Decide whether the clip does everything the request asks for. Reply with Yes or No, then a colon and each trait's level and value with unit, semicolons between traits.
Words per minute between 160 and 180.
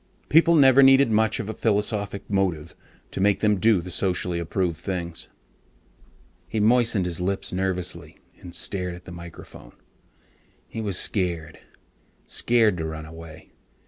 No: average, 145 wpm